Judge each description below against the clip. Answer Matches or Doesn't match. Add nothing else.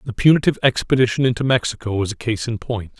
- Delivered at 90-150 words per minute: Doesn't match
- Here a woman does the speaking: Doesn't match